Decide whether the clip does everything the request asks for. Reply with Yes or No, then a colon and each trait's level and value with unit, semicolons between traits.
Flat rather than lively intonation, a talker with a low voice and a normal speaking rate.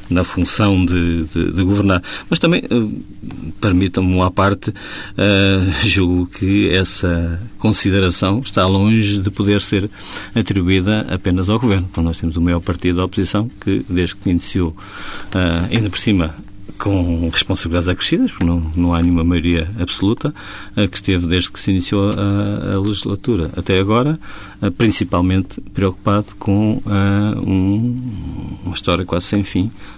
Yes: narrow, 2.3 semitones; very low, 95 Hz; average, 150 wpm